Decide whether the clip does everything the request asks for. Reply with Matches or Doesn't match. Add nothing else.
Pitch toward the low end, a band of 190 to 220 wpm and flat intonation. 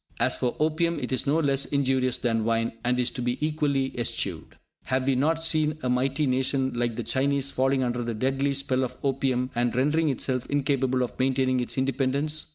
Matches